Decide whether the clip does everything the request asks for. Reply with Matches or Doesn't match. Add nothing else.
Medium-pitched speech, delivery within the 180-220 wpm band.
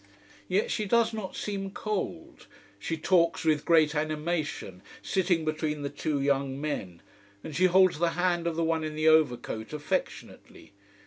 Doesn't match